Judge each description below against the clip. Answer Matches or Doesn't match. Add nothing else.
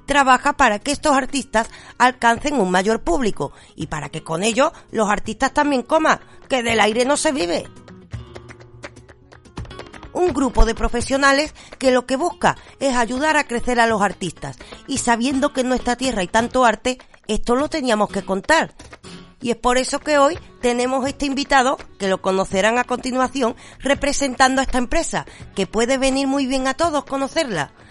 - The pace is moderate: Matches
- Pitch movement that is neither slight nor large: Matches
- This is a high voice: Matches